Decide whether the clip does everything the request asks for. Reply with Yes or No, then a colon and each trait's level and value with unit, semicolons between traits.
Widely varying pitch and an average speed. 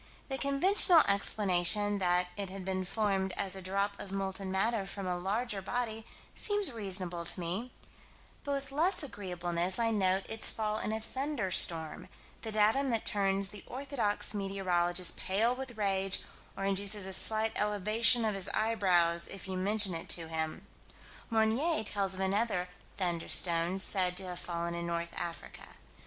No: average, 3.2 semitones; average, 160 wpm